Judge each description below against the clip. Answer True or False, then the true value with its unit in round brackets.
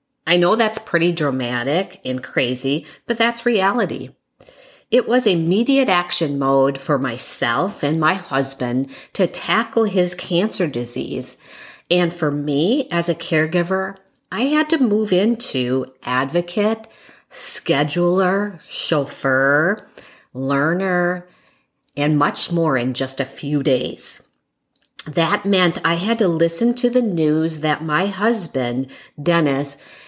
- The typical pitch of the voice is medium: True (170 Hz)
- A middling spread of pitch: False (6.0 semitones)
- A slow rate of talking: True (120 wpm)